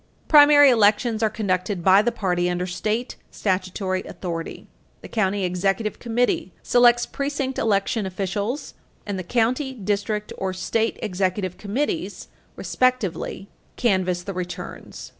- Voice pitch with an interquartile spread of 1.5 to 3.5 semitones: No, average, 4.3 semitones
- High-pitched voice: Yes, high, 205 Hz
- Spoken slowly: Yes, slow, 120 wpm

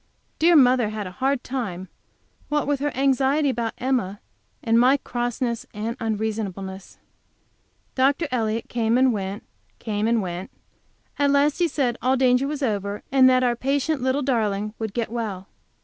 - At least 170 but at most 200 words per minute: No, average, 160 wpm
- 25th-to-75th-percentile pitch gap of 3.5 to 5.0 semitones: Yes, average, 3.9 semitones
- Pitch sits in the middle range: No, high, 240 Hz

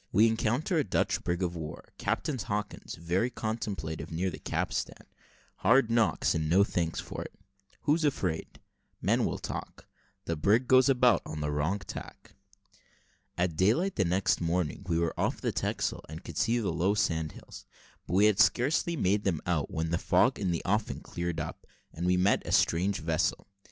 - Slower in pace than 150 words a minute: No, average, 180 wpm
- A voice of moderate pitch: No, very low, 95 Hz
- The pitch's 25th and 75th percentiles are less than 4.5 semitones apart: No, average, 5.1 semitones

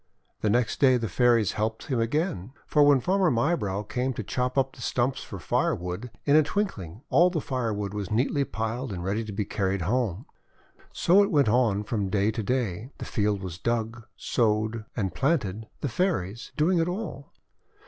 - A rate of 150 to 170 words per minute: No, average, 190 wpm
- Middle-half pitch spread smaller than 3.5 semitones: No, average, 4.9 semitones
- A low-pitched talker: Yes, low, 115 Hz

